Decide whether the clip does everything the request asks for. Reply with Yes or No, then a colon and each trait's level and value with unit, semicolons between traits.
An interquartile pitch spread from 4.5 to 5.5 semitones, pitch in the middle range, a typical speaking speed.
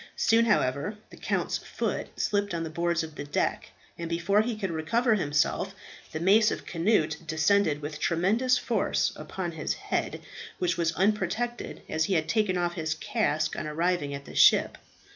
Yes: average, 4.9 semitones; medium, 175 Hz; average, 175 wpm